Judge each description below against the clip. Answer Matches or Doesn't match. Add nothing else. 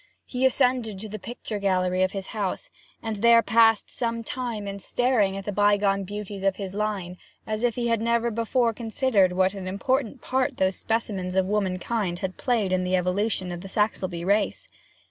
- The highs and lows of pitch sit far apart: Doesn't match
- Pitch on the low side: Doesn't match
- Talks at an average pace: Matches